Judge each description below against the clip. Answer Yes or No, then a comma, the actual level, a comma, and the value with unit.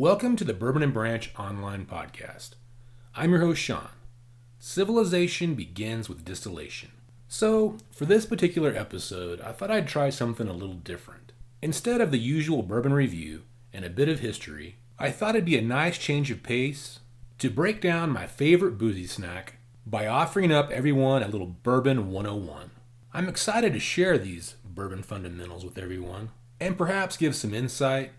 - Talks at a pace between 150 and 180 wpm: Yes, average, 165 wpm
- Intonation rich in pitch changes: Yes, wide, 6.1 semitones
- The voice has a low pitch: Yes, low, 120 Hz